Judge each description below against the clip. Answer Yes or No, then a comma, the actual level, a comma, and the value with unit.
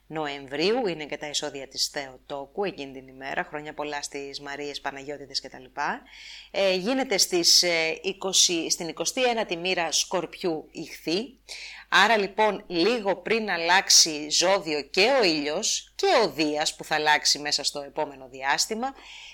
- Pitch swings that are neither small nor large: Yes, average, 4.9 semitones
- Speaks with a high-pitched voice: No, medium, 155 Hz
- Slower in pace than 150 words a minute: Yes, average, 140 wpm